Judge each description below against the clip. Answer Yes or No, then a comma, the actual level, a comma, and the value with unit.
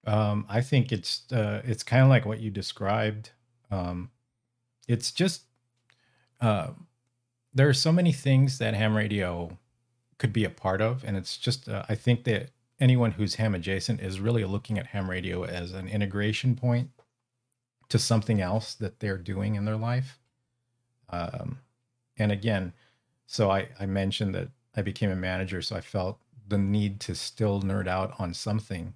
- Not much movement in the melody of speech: No, average, 3.5 semitones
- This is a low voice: Yes, low, 110 Hz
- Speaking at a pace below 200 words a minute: Yes, average, 170 wpm